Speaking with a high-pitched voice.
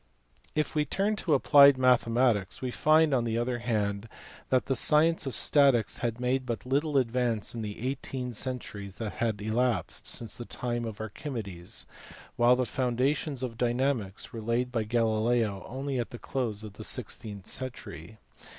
No: low, 120 Hz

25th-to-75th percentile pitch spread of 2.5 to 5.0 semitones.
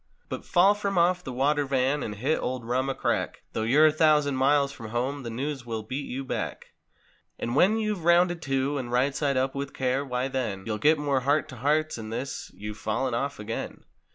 Yes: average, 3.1 semitones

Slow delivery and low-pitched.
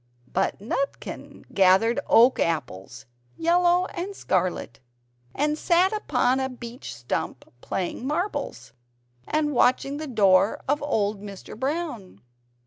No: slow, 115 wpm; very high, 255 Hz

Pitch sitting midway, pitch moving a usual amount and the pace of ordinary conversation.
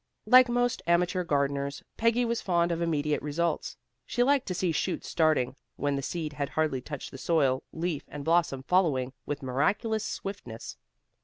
Yes: medium, 160 Hz; average, 4.7 semitones; average, 165 wpm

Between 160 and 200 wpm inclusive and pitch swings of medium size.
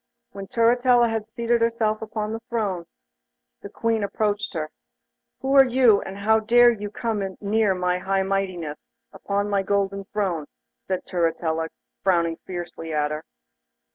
No: average, 145 wpm; average, 3.6 semitones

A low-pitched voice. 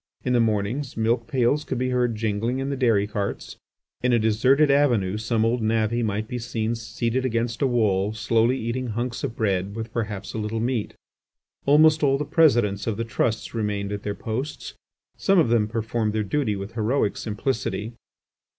Yes: low, 115 Hz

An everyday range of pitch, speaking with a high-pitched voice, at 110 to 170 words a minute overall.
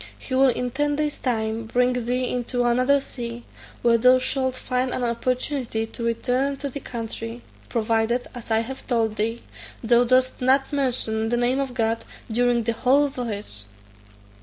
No: narrow, 2.0 semitones; high, 245 Hz; average, 165 wpm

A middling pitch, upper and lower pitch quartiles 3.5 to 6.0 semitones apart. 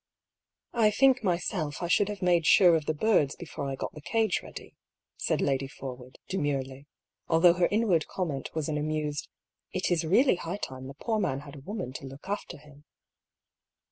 Yes: medium, 160 Hz; average, 5.3 semitones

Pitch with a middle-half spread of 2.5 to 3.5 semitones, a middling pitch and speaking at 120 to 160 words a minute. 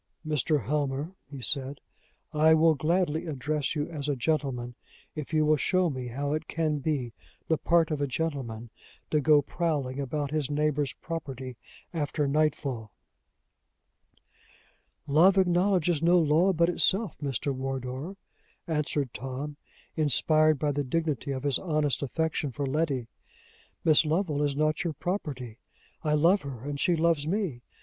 Yes: average, 2.8 semitones; medium, 150 Hz; average, 145 wpm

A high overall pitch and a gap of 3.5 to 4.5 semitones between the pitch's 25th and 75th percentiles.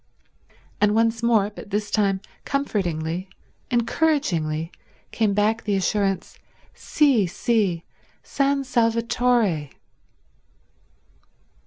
Yes: high, 210 Hz; average, 3.8 semitones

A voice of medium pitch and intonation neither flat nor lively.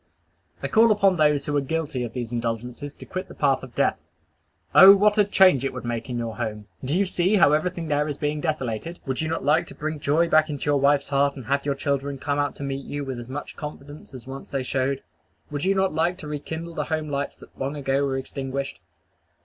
Yes: medium, 145 Hz; average, 3.0 semitones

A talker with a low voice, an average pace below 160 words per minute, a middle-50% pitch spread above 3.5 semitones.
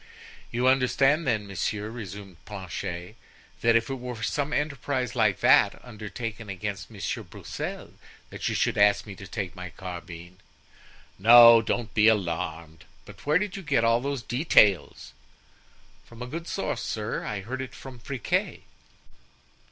Yes: low, 115 Hz; average, 150 wpm; average, 4.4 semitones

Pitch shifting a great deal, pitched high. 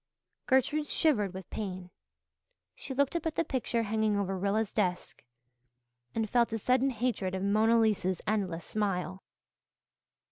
No: average, 4.6 semitones; high, 215 Hz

